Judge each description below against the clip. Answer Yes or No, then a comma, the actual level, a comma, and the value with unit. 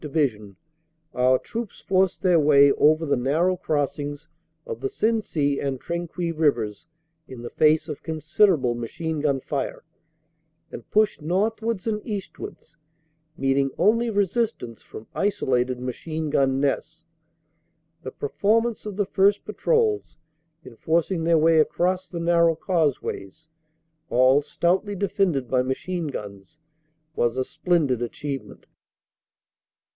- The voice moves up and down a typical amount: No, wide, 5.7 semitones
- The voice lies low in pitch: No, medium, 160 Hz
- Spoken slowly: Yes, slow, 125 wpm